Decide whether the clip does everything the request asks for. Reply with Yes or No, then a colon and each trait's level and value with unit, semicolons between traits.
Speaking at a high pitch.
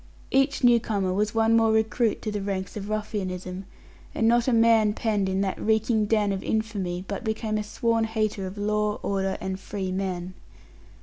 Yes: high, 210 Hz